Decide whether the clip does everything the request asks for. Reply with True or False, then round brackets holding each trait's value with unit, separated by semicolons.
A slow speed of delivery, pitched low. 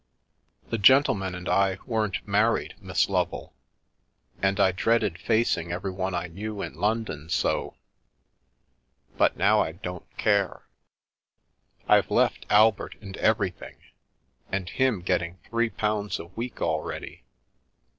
True (120 wpm; 100 Hz)